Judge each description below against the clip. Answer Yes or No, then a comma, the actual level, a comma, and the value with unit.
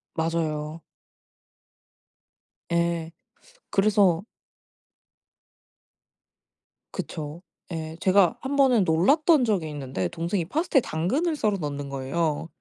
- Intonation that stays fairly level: No, average, 5.1 semitones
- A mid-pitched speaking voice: Yes, medium, 170 Hz